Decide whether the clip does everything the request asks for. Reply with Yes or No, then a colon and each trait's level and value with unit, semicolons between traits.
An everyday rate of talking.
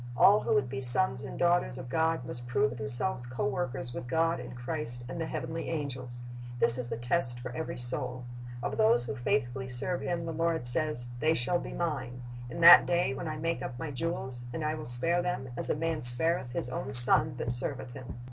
No: fast, 215 wpm